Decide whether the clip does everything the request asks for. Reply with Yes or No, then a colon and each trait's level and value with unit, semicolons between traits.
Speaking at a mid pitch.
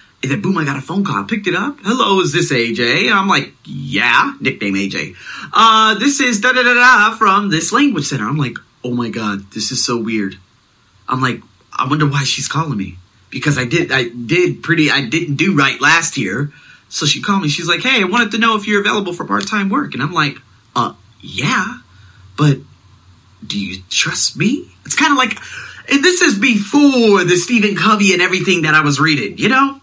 Yes: medium, 165 Hz